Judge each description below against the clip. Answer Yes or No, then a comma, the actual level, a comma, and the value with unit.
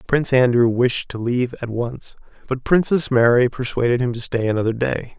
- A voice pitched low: Yes, low, 125 Hz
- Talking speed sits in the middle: Yes, average, 185 wpm